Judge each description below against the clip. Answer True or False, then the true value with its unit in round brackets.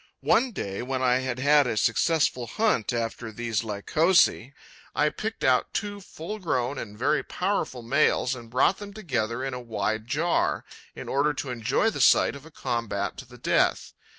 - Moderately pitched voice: False (130 Hz)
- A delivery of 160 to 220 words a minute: True (180 wpm)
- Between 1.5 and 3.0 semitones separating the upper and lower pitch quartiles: False (5.2 semitones)